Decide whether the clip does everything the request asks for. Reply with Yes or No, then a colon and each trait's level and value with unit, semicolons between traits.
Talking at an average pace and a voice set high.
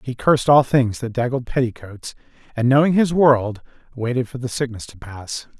No: average, 180 wpm; low, 125 Hz